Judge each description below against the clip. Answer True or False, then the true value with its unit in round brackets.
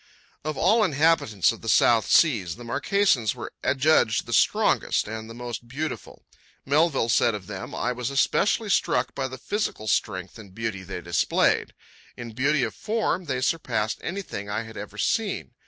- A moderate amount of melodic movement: False (6.1 semitones)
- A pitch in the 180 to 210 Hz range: False (120 Hz)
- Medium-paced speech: True (170 wpm)